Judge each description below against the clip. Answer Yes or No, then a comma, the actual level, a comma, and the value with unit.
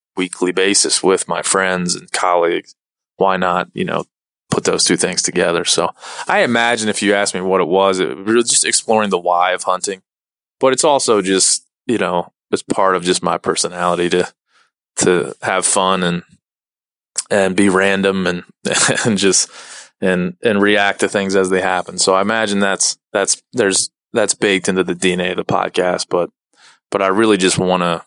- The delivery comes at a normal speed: Yes, average, 185 wpm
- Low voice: Yes, very low, 95 Hz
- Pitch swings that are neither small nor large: No, narrow, 1.7 semitones